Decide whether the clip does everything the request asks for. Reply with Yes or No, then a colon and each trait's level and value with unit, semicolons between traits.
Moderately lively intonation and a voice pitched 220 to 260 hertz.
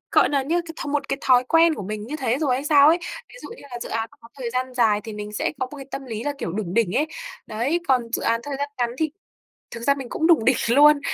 Yes: average, 4.1 semitones; very high, 255 Hz